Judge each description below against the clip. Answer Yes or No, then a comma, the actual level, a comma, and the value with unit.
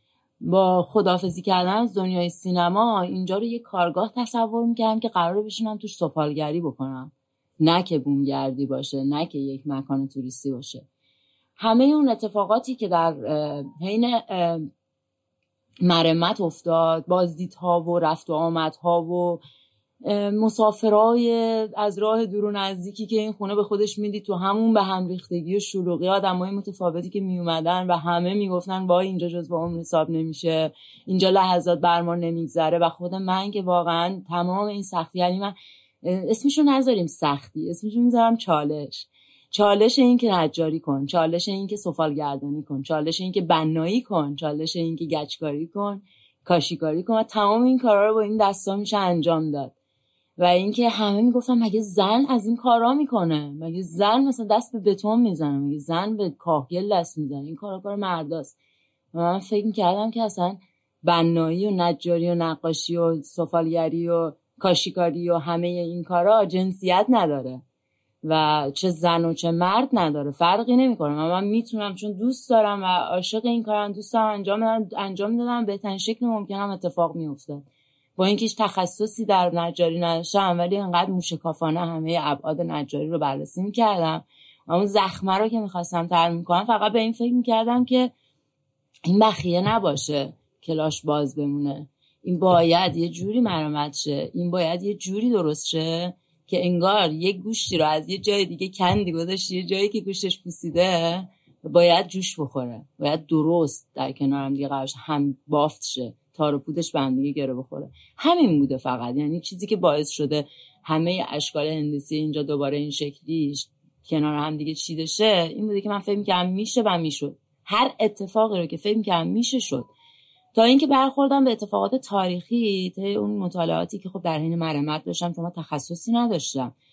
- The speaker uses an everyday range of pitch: Yes, average, 4.8 semitones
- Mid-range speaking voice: Yes, medium, 175 Hz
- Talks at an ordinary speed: No, fast, 160 wpm